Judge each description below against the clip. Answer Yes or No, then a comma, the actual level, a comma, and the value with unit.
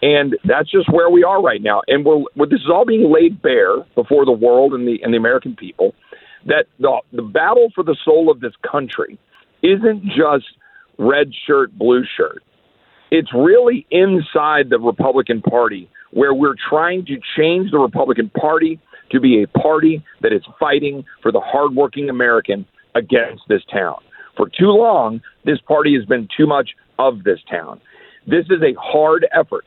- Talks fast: No, average, 175 wpm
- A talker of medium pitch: Yes, medium, 155 Hz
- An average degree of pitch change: No, wide, 6.4 semitones